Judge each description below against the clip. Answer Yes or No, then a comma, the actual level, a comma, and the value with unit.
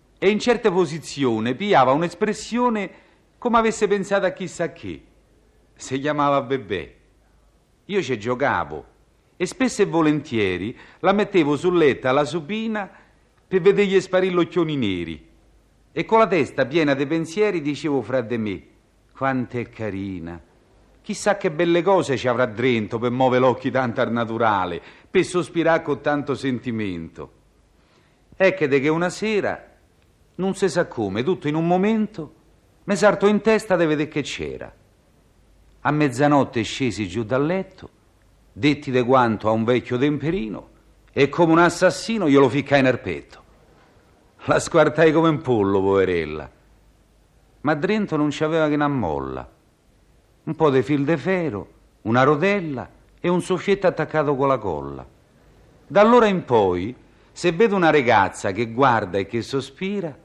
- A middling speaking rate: Yes, average, 150 wpm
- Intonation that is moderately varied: No, wide, 6.8 semitones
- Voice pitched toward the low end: No, medium, 150 Hz